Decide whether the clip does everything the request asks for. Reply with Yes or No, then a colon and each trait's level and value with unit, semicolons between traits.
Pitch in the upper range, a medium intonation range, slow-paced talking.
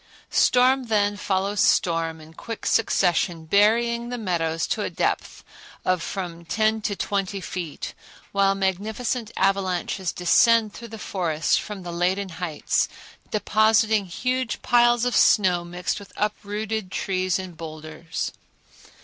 Yes: high, 195 Hz; average, 3.8 semitones; slow, 130 wpm